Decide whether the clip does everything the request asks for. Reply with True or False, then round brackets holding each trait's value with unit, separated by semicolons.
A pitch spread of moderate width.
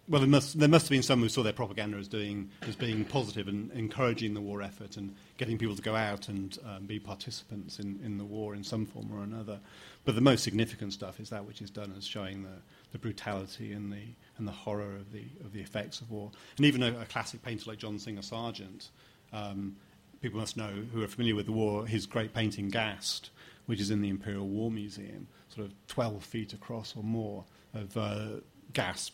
False (1.9 semitones)